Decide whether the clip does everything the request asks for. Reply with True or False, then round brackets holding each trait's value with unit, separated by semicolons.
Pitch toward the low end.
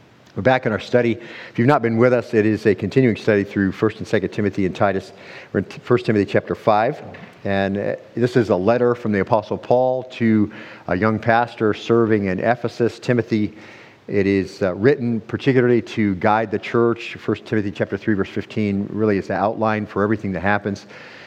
True (110 Hz)